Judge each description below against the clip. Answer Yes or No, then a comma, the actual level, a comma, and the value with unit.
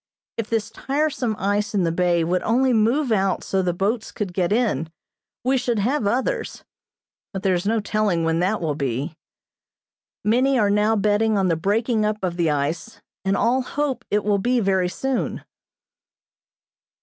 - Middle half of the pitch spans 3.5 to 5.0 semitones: Yes, average, 4.3 semitones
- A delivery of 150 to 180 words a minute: Yes, average, 175 wpm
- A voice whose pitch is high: Yes, high, 210 Hz